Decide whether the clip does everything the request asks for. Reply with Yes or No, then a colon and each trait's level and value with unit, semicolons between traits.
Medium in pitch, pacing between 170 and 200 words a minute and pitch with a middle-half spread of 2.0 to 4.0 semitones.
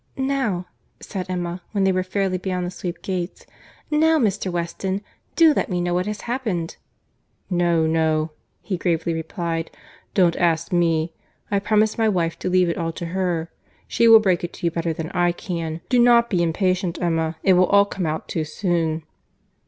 Yes: medium, 180 Hz; average, 175 wpm; average, 2.9 semitones